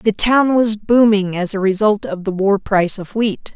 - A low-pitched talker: No, high, 205 Hz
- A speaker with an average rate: No, fast, 220 wpm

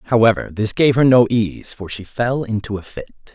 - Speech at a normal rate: No, fast, 215 wpm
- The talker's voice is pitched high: No, low, 110 Hz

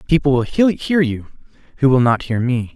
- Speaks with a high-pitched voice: No, low, 135 Hz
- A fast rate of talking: No, average, 195 wpm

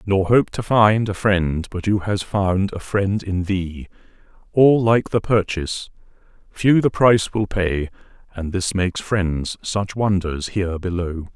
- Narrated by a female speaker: No, male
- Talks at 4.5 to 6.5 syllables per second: No, 4.1 syllables/s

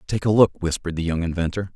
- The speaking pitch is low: Yes, very low, 90 Hz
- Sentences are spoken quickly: Yes, fast, 240 wpm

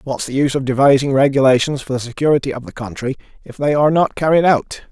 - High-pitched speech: No, medium, 140 Hz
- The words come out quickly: Yes, fast, 220 wpm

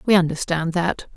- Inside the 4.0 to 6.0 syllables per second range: Yes, 5.1 syllables/s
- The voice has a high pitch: No, medium, 170 Hz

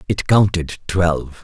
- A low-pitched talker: Yes, very low, 85 Hz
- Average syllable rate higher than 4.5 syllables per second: No, 4.2 syllables/s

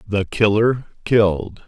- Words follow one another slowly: Yes, slow, 105 wpm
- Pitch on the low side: Yes, low, 105 Hz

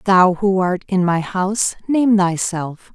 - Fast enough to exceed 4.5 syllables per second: No, 3.8 syllables/s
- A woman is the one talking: Yes, female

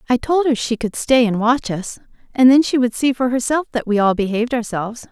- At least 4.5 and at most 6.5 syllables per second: Yes, 5.8 syllables/s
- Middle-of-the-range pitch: No, high, 245 Hz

